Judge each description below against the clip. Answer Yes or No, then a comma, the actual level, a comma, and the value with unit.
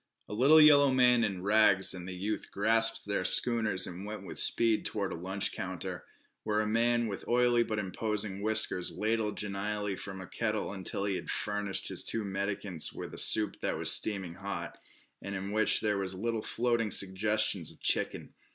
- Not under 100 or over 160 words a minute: No, average, 185 wpm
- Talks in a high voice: No, low, 105 Hz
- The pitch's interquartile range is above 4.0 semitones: No, narrow, 2.6 semitones